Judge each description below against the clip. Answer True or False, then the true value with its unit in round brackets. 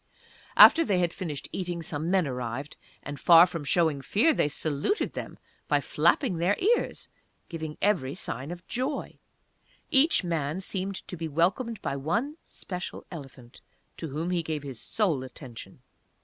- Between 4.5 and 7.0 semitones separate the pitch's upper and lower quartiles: True (5.0 semitones)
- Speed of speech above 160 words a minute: False (155 wpm)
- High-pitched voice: False (170 Hz)